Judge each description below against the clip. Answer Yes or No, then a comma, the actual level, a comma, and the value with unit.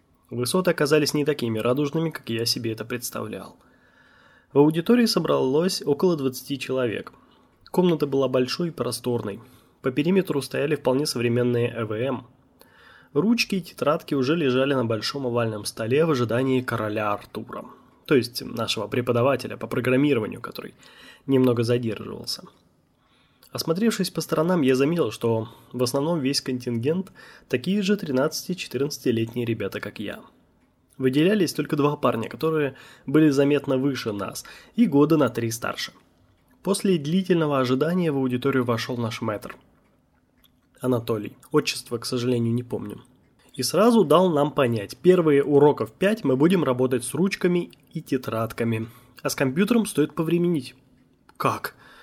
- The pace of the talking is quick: No, average, 130 wpm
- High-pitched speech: No, low, 135 Hz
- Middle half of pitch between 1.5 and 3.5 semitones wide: No, average, 4.6 semitones